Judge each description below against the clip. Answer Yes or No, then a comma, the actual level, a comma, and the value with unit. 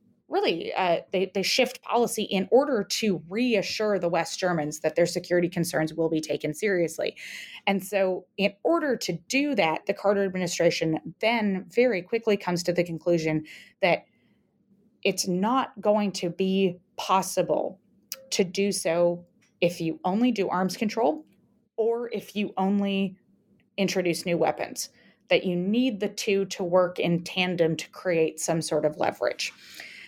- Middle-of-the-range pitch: No, high, 195 Hz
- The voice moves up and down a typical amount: Yes, average, 3.6 semitones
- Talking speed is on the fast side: No, average, 150 wpm